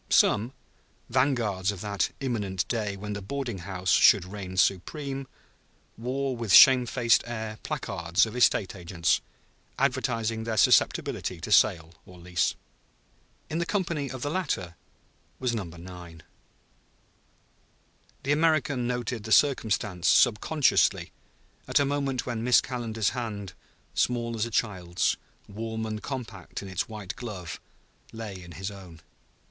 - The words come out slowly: Yes, slow, 130 wpm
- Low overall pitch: Yes, low, 110 Hz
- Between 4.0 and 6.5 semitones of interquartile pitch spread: Yes, average, 4.8 semitones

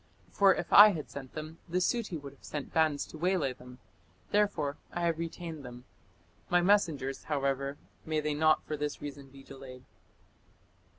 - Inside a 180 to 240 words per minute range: No, average, 170 wpm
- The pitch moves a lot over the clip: No, average, 3.7 semitones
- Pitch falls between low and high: Yes, medium, 150 Hz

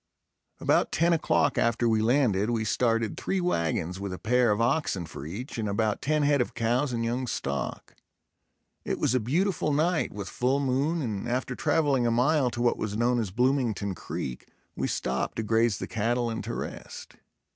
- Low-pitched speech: Yes, low, 120 Hz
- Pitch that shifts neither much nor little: Yes, average, 4.1 semitones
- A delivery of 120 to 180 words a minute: No, average, 190 wpm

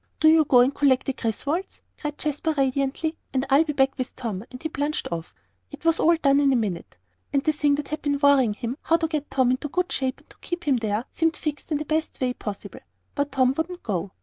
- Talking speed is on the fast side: Yes, fast, 245 wpm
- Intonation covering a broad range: No, average, 3.3 semitones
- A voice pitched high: Yes, very high, 285 Hz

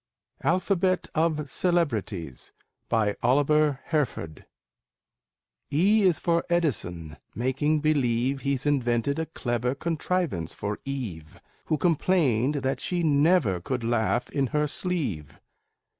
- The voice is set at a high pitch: No, medium, 140 Hz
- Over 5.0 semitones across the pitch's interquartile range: Yes, wide, 5.6 semitones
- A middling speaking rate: No, slow, 110 wpm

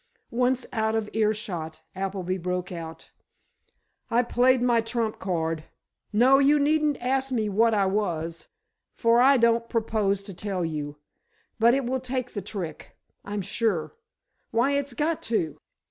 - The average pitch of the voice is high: Yes, high, 220 Hz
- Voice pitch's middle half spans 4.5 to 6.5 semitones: Yes, average, 4.8 semitones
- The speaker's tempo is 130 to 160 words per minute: Yes, average, 145 wpm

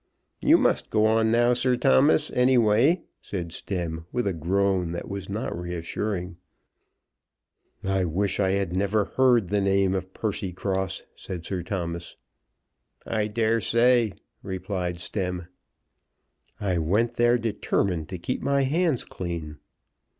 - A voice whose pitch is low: Yes, low, 100 Hz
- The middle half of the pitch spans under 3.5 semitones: No, average, 4.3 semitones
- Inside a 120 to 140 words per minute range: Yes, slow, 135 wpm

